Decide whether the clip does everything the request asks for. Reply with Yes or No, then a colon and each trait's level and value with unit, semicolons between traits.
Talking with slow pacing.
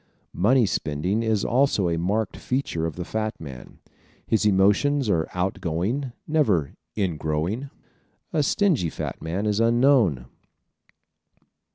Yes: slow, 130 wpm